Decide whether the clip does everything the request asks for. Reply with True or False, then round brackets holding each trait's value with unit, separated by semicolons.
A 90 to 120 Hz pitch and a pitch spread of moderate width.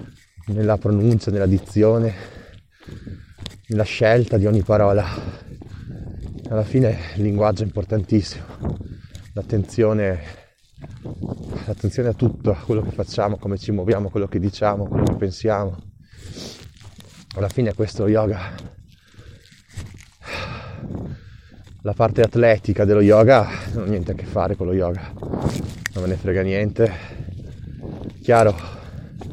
False (105 Hz; 2.2 semitones)